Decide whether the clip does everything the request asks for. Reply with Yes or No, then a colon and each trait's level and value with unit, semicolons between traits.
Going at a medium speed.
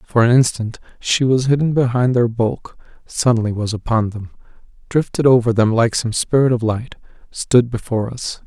Yes: average, 170 wpm